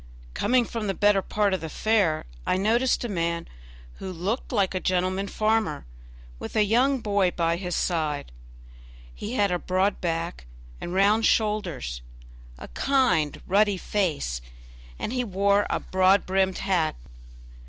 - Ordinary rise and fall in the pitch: Yes, average, 3.4 semitones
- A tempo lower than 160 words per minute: Yes, average, 150 wpm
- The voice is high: Yes, high, 195 Hz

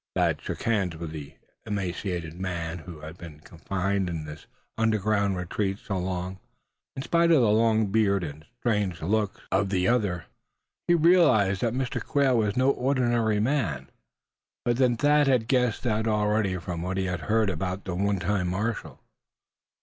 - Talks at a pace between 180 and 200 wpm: No, average, 165 wpm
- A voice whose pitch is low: Yes, low, 100 Hz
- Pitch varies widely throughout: No, average, 4.2 semitones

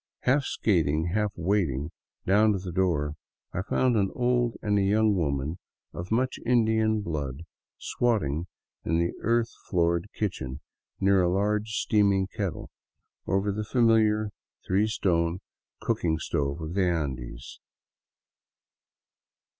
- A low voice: Yes, very low, 95 Hz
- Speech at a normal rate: No, slow, 125 wpm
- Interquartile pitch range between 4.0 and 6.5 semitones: Yes, average, 4.6 semitones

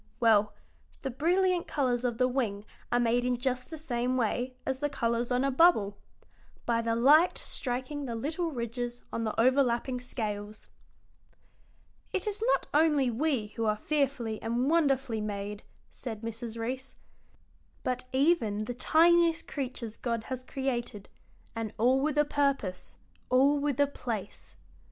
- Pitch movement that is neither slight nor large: Yes, average, 3.6 semitones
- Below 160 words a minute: Yes, average, 150 wpm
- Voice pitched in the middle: No, very high, 250 Hz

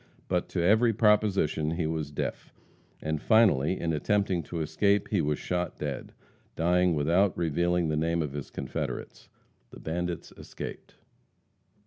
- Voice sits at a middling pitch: No, very low, 85 Hz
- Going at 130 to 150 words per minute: Yes, average, 140 wpm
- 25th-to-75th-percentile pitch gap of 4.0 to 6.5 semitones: No, average, 3.6 semitones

